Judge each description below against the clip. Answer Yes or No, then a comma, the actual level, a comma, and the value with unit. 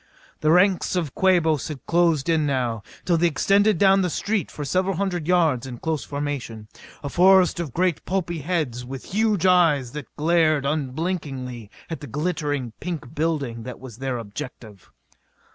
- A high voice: No, medium, 155 Hz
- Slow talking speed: No, average, 160 wpm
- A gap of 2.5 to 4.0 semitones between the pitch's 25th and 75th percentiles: No, average, 5.2 semitones